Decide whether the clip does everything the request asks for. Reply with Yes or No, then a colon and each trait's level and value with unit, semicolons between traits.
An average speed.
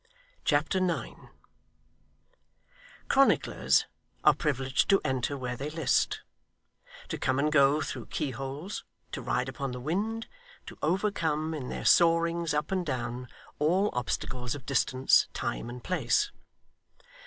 No: slow, 125 wpm